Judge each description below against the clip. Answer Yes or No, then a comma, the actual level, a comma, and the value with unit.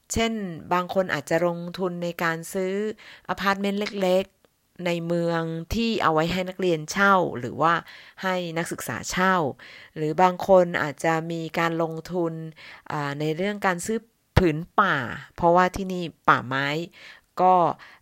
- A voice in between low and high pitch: Yes, medium, 175 Hz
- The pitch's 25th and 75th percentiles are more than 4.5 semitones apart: No, narrow, 2.4 semitones